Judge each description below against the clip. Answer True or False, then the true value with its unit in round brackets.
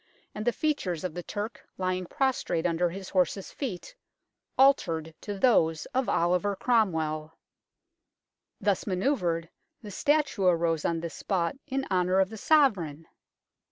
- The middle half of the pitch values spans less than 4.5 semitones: False (5.3 semitones)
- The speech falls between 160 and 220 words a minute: False (135 wpm)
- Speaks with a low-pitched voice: False (185 Hz)